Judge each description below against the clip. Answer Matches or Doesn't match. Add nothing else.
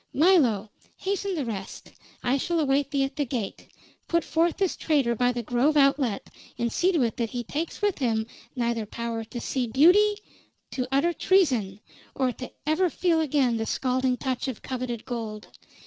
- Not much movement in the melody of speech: Doesn't match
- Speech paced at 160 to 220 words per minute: Matches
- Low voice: Doesn't match